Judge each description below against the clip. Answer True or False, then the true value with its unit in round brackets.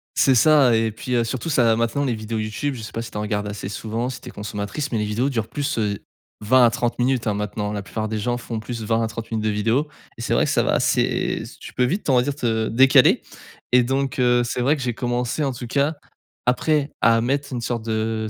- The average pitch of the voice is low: True (115 Hz)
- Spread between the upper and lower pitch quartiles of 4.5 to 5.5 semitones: False (3.0 semitones)